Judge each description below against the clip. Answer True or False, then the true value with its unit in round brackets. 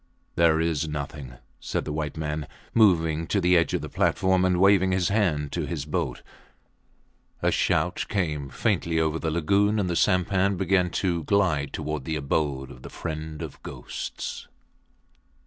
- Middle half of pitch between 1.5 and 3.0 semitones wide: False (3.5 semitones)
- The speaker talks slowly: False (165 wpm)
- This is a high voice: False (80 Hz)